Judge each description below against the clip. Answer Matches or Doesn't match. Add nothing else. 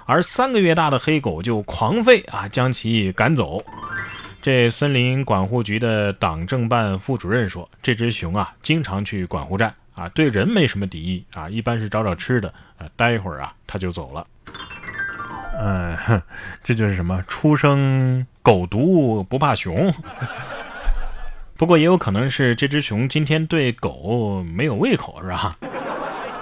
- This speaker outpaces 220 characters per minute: Matches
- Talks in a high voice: Doesn't match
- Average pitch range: Doesn't match